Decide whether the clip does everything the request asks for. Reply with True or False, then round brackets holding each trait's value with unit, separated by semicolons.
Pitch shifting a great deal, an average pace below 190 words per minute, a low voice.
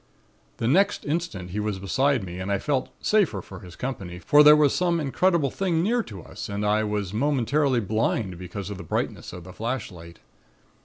False (7.6 semitones; 195 wpm; 110 Hz)